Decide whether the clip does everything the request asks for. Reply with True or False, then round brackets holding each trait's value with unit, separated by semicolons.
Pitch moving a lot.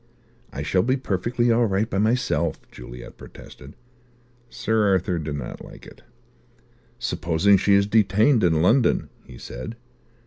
True (5.7 semitones)